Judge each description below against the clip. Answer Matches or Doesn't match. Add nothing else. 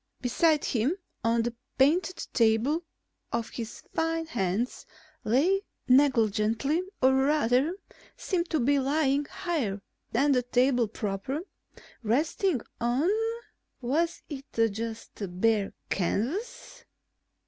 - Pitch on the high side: Matches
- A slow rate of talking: Matches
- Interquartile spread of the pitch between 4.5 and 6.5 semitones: Matches